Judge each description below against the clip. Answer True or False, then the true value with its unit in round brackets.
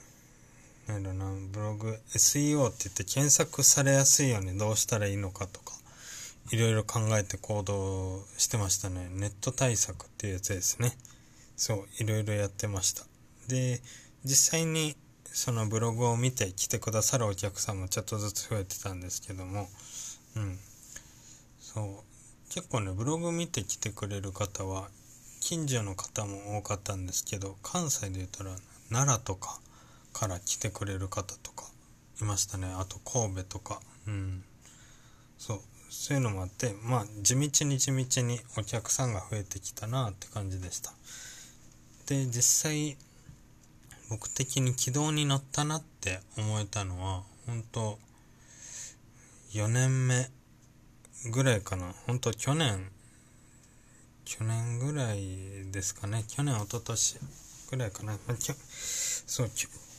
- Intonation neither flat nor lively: True (4.0 semitones)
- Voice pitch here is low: True (110 Hz)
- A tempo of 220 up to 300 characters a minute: True (270 characters per minute)